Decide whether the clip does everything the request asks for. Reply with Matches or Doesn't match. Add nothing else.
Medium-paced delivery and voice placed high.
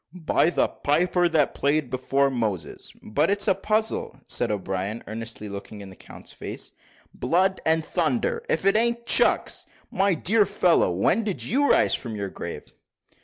Doesn't match